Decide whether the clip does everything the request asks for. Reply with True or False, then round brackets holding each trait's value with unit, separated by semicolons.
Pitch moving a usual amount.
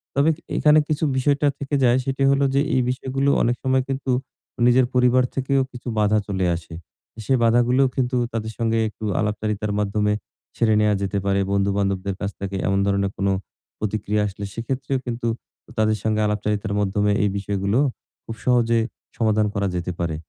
True (4.1 semitones)